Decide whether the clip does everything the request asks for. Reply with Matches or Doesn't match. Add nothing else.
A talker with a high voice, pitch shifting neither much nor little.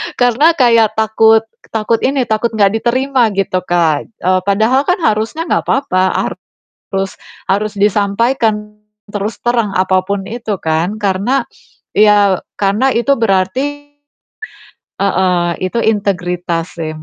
Matches